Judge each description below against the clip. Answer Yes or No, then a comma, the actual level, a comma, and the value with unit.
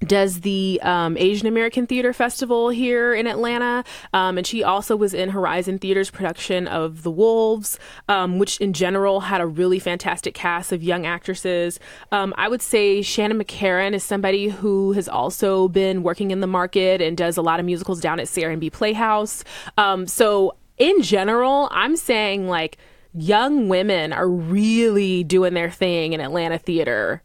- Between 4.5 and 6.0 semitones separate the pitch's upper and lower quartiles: No, average, 3.1 semitones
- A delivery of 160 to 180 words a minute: Yes, average, 170 wpm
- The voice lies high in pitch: Yes, high, 195 Hz